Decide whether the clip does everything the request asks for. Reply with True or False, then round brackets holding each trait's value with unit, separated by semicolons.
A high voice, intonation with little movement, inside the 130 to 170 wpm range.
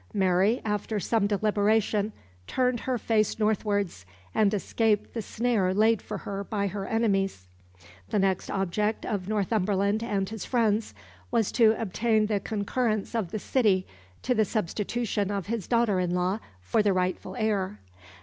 True (210 Hz; 2.3 semitones; 150 wpm)